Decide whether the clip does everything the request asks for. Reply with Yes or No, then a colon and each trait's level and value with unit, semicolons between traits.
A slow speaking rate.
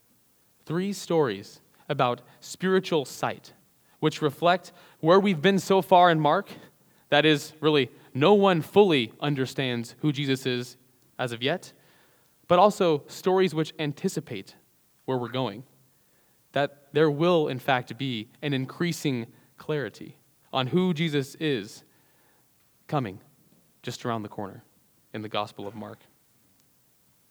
Yes: slow, 125 wpm